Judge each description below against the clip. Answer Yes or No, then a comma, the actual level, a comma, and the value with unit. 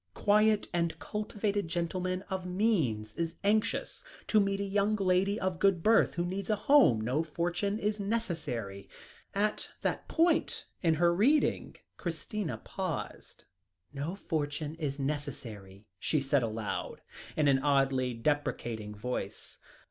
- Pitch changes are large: Yes, wide, 6.5 semitones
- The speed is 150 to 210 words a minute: No, slow, 135 wpm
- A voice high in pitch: No, medium, 170 Hz